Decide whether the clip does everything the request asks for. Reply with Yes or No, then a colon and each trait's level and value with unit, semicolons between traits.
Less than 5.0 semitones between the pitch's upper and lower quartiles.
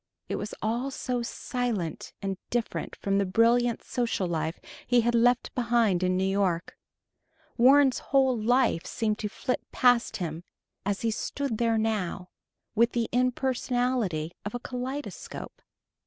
Yes: average, 3.9 semitones